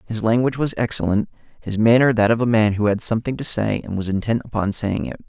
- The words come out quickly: Yes, fast, 240 wpm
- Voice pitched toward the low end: Yes, low, 110 Hz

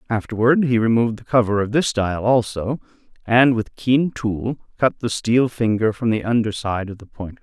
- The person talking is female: No, male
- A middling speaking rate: Yes, average, 195 wpm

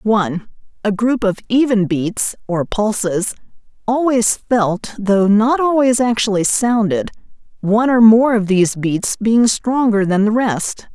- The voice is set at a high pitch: Yes, high, 215 Hz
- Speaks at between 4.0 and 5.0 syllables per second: Yes, 4.2 syllables/s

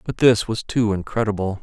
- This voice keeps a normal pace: Yes, average, 185 wpm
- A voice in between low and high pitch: No, low, 105 Hz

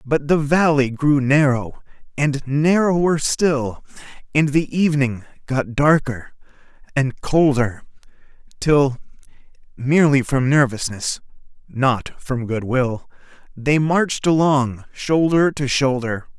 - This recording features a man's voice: Yes, male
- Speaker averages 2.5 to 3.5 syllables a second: Yes, 3.4 syllables/s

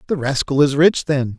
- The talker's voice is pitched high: No, medium, 145 Hz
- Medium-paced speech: No, fast, 215 wpm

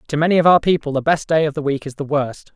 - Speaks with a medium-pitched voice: Yes, medium, 150 Hz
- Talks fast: Yes, fast, 330 wpm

